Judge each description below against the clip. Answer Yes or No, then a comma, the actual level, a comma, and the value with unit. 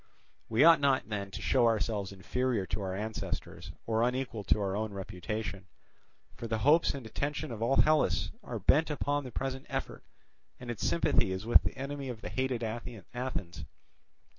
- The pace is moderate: Yes, average, 175 wpm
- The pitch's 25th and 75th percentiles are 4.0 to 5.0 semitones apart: Yes, average, 4.5 semitones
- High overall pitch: No, low, 115 Hz